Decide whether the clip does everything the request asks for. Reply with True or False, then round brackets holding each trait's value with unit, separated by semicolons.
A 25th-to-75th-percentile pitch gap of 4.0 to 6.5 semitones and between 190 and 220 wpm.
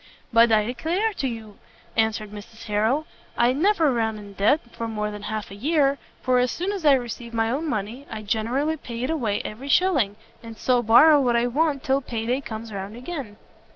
True (4.4 semitones; 205 wpm)